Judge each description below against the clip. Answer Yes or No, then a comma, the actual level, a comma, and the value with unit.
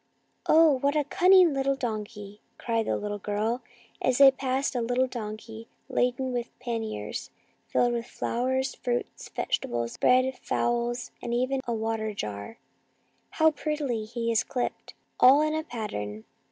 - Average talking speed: Yes, average, 155 wpm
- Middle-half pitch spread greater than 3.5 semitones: No, average, 3.2 semitones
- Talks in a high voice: Yes, high, 240 Hz